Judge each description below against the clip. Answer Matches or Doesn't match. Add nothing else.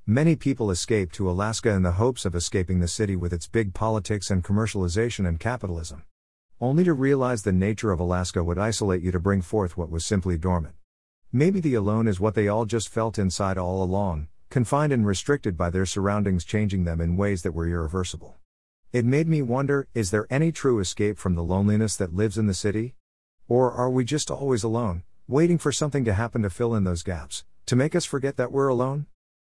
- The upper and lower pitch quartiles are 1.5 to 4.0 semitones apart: Doesn't match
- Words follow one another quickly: Matches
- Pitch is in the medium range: Doesn't match